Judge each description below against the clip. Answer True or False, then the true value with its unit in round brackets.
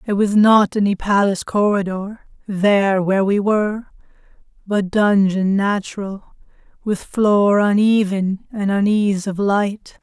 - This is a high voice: True (200 Hz)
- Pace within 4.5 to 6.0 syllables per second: False (4.2 syllables/s)